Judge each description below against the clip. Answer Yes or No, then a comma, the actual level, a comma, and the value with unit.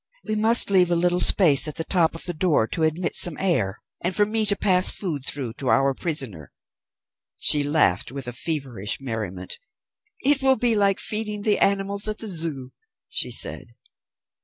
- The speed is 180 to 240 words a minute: Yes, average, 185 wpm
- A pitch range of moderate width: No, wide, 6.7 semitones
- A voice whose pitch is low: No, medium, 170 Hz